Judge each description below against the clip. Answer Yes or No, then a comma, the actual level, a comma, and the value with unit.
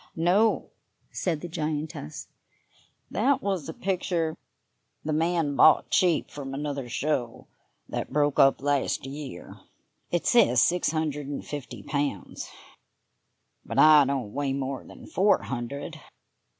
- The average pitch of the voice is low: No, medium, 150 Hz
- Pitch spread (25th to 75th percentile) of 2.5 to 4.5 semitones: Yes, average, 3.4 semitones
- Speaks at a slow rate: Yes, slow, 125 wpm